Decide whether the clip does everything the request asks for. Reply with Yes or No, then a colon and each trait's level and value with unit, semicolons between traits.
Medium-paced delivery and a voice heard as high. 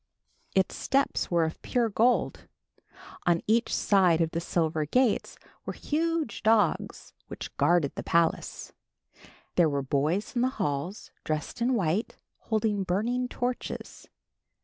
No: slow, 130 wpm; high, 195 Hz